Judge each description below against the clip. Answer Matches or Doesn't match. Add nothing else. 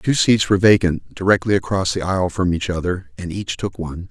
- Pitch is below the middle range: Matches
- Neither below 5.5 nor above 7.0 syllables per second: Matches